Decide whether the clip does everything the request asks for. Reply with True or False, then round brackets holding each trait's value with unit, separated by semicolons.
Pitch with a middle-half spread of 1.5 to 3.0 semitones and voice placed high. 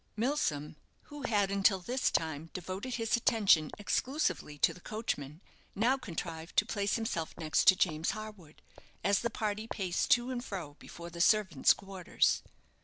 False (5.2 semitones; 195 Hz)